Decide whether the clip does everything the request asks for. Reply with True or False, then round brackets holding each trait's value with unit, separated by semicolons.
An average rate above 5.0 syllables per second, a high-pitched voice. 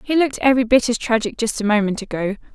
True (7.0 syllables/s; 235 Hz)